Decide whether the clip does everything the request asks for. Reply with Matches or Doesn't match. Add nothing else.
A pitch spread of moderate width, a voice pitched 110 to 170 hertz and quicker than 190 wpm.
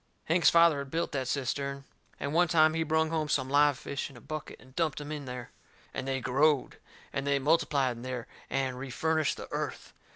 Matches